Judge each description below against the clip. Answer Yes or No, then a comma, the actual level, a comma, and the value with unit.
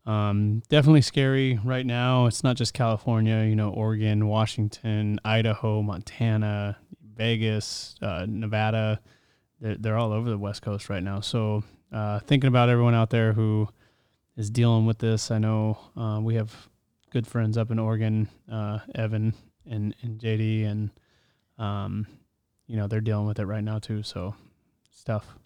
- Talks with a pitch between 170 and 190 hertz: No, low, 110 Hz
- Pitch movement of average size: No, narrow, 1.3 semitones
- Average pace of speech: Yes, average, 160 wpm